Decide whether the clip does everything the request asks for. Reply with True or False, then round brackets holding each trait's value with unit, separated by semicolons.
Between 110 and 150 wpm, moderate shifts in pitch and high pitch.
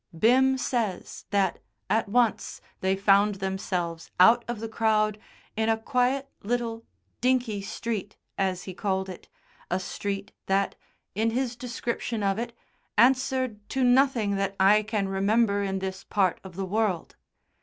True (145 wpm; 3.4 semitones; 210 Hz)